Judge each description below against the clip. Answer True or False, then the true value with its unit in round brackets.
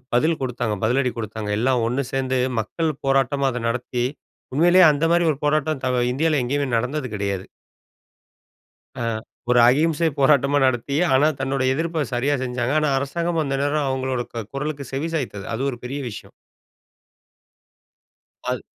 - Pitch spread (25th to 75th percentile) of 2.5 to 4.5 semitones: True (3.4 semitones)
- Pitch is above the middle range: False (135 Hz)